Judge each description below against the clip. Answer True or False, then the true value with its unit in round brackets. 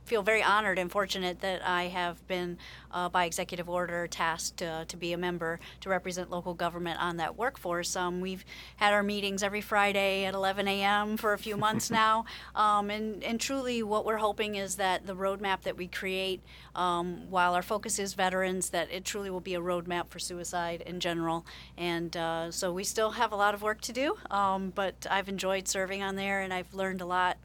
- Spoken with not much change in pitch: True (2.3 semitones)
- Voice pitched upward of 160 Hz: True (190 Hz)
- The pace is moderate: False (210 wpm)